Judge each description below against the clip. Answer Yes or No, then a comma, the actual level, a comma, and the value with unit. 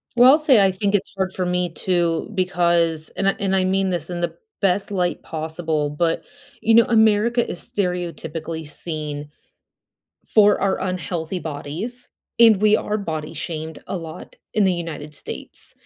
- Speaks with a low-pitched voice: No, medium, 180 Hz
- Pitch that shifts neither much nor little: Yes, average, 3.8 semitones